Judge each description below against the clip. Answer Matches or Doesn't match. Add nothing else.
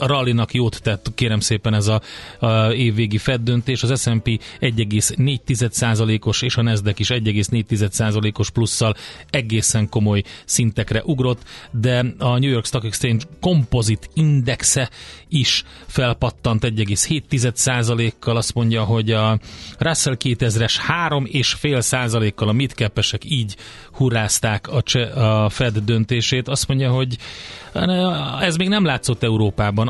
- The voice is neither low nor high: Doesn't match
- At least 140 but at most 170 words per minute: Doesn't match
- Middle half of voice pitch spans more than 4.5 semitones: Doesn't match